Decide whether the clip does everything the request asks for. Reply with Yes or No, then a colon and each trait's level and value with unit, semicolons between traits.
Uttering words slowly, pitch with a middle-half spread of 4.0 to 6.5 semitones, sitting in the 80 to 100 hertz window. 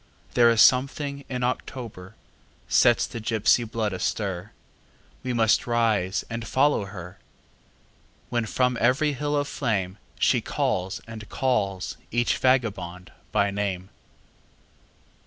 No: slow, 120 wpm; average, 4.3 semitones; low, 115 Hz